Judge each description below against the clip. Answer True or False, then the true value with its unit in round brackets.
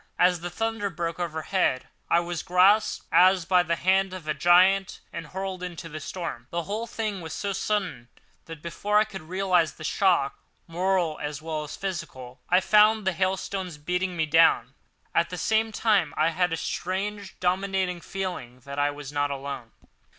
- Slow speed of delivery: False (180 wpm)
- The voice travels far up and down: False (3.4 semitones)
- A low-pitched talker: False (180 Hz)